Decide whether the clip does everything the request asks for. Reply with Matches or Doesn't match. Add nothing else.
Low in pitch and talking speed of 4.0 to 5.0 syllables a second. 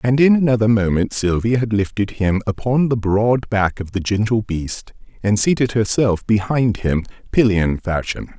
Matches